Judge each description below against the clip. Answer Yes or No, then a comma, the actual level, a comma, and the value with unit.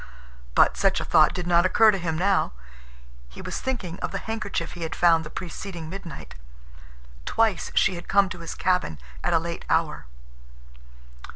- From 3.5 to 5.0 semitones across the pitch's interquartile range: No, average, 3.0 semitones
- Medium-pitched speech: Yes, medium, 175 Hz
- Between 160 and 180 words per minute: Yes, average, 175 wpm